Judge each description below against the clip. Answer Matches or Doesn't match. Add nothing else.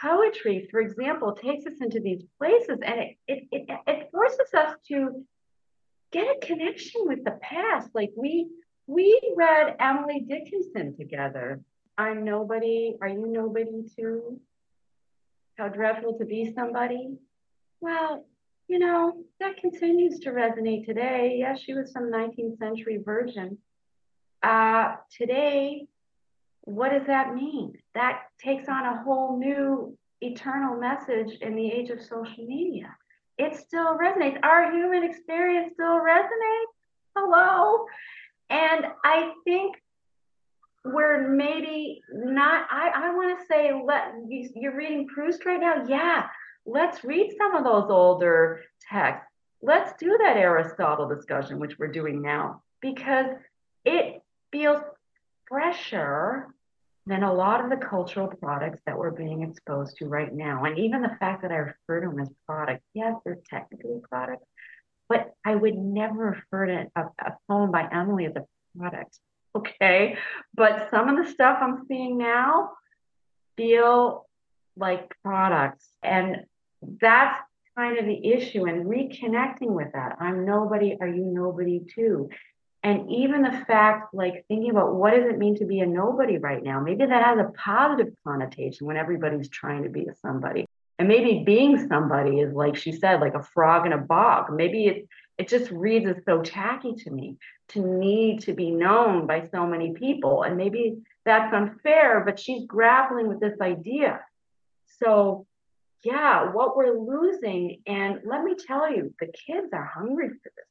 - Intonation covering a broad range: Matches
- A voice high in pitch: Matches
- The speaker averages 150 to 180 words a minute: Matches